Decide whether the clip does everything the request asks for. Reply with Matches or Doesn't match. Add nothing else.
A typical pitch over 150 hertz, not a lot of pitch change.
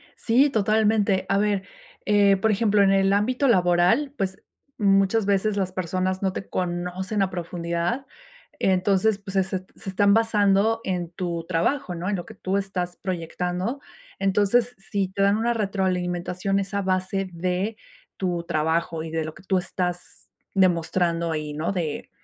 Matches